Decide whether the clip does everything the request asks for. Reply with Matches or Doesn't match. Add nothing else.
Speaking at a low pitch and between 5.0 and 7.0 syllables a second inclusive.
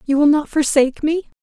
Doesn't match